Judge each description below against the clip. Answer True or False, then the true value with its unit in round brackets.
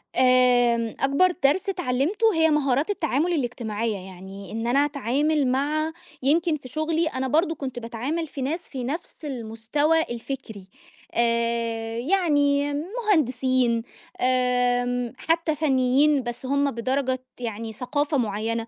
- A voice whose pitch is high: True (260 Hz)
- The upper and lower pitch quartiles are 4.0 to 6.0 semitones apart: True (4.3 semitones)